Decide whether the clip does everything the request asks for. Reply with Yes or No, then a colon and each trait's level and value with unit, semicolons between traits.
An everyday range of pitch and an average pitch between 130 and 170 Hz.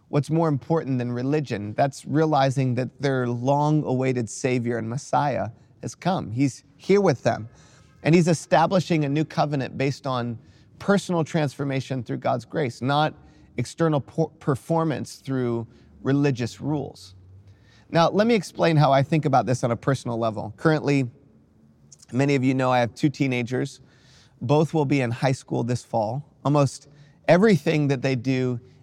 Yes: average, 3.6 semitones; low, 135 Hz